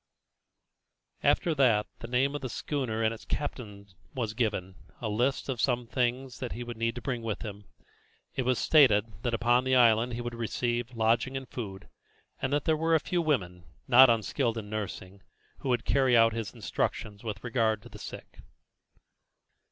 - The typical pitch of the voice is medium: No, low, 120 Hz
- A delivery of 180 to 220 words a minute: Yes, average, 190 wpm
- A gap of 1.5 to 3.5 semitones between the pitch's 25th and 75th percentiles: Yes, average, 2.9 semitones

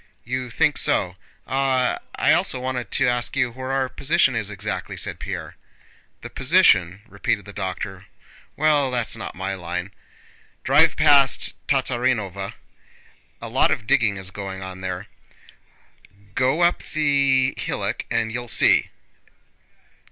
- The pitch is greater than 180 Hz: No, low, 120 Hz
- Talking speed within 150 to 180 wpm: No, slow, 135 wpm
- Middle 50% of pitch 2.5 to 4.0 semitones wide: No, wide, 5.5 semitones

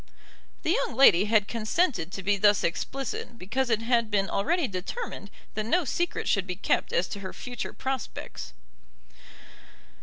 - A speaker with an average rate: Yes, average, 155 wpm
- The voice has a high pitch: Yes, high, 220 Hz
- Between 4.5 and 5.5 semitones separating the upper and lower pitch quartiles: Yes, average, 5.0 semitones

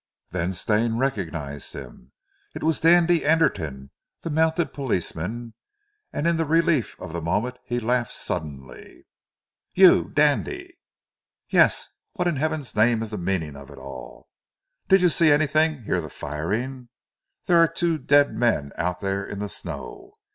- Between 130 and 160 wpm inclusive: Yes, average, 150 wpm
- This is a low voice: Yes, low, 120 Hz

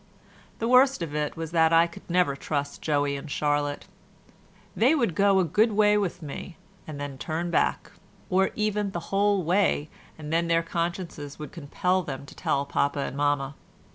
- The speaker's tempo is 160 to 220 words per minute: Yes, average, 180 wpm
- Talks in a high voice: No, medium, 165 Hz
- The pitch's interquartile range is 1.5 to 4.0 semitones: No, average, 4.8 semitones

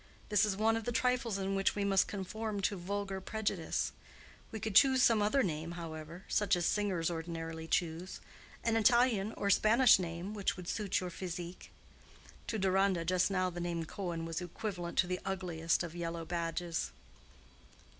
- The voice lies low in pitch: No, medium, 185 Hz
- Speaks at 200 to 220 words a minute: No, average, 165 wpm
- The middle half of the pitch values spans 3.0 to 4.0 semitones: Yes, average, 3.5 semitones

